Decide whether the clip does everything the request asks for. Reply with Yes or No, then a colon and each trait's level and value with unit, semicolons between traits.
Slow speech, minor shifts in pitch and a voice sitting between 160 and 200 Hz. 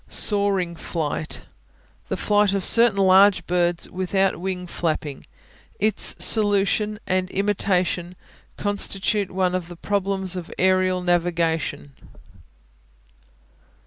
Yes: slow, 100 wpm; narrow, 2.2 semitones; medium, 185 Hz